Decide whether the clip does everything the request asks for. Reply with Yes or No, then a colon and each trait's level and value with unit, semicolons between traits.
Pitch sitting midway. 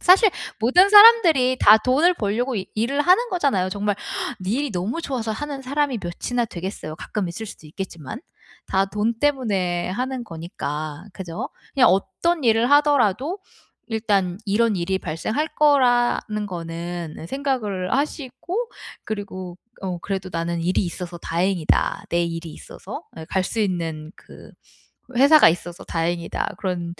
No: high, 205 Hz